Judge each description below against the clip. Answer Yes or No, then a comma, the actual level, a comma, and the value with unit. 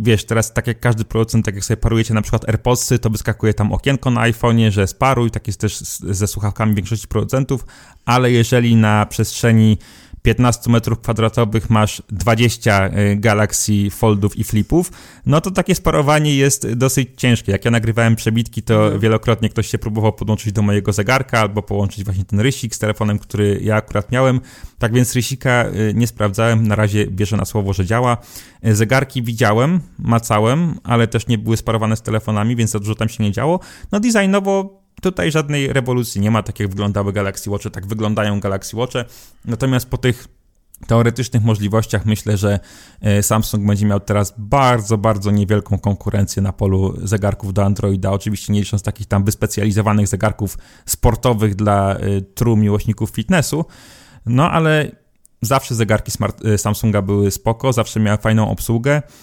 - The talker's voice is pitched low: Yes, low, 110 Hz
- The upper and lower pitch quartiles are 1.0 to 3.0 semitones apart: Yes, narrow, 2.6 semitones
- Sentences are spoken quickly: Yes, fast, 165 wpm